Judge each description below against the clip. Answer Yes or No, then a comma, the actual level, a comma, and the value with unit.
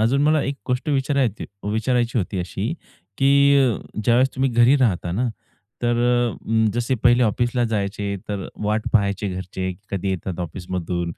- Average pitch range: Yes, average, 4.4 semitones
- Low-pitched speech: Yes, low, 115 Hz